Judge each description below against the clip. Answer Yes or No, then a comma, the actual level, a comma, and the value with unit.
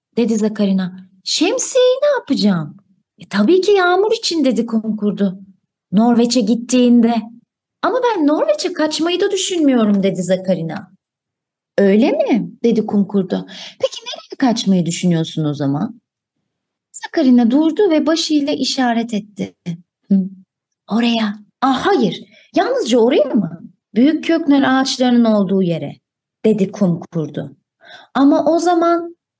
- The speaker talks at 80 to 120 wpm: Yes, average, 110 wpm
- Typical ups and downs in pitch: No, wide, 7.9 semitones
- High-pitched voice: Yes, high, 230 Hz